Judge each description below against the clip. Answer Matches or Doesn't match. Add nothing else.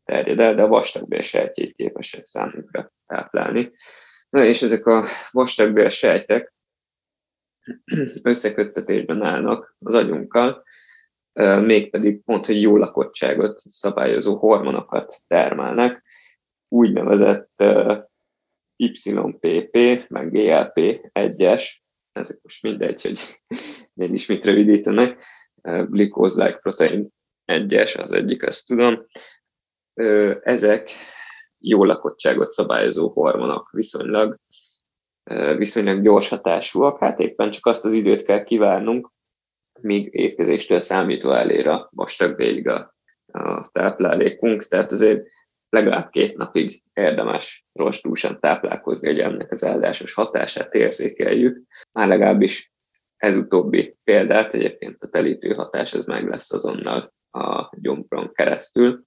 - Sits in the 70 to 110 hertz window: Doesn't match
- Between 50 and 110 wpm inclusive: Matches